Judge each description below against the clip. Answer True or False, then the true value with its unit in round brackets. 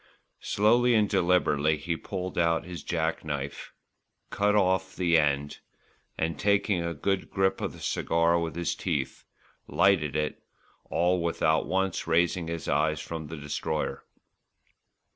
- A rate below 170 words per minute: True (140 wpm)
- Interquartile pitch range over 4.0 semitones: False (3.1 semitones)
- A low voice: True (85 Hz)